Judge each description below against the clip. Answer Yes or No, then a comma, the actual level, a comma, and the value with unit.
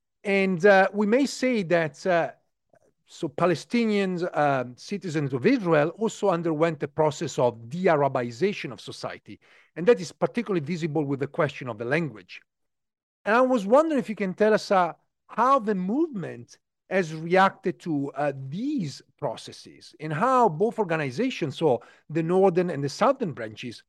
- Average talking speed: Yes, average, 160 wpm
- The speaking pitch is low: No, medium, 175 Hz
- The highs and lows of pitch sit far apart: Yes, wide, 6.0 semitones